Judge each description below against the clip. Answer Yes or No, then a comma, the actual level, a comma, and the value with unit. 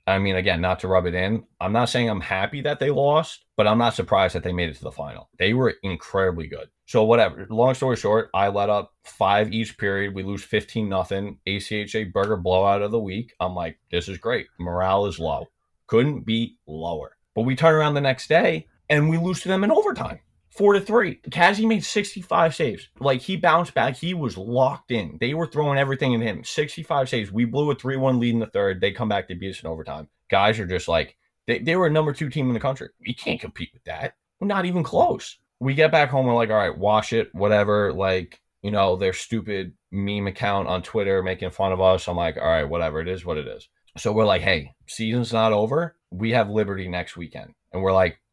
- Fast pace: Yes, fast, 235 wpm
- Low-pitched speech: Yes, low, 110 Hz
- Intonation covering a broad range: Yes, wide, 6.4 semitones